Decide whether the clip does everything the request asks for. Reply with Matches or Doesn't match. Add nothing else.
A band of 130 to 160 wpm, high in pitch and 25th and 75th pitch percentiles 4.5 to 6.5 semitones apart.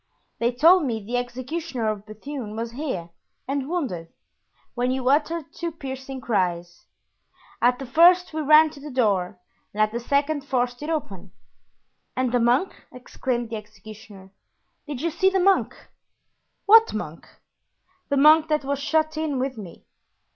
Matches